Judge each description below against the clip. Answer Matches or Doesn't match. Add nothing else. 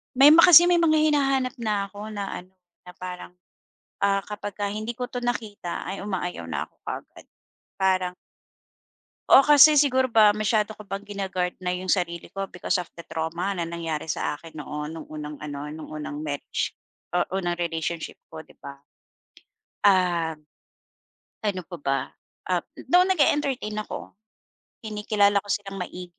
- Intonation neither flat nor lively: Matches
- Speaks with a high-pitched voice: Matches